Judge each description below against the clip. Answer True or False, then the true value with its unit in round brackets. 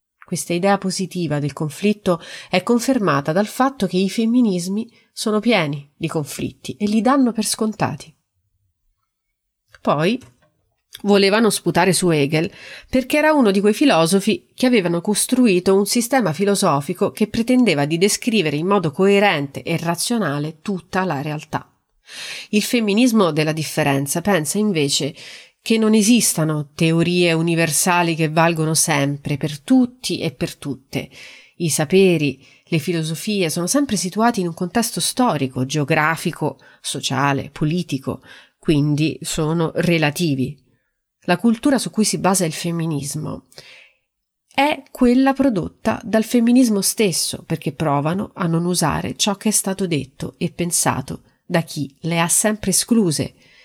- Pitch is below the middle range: False (175 Hz)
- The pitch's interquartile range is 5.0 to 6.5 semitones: True (5.3 semitones)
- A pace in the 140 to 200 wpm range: False (130 wpm)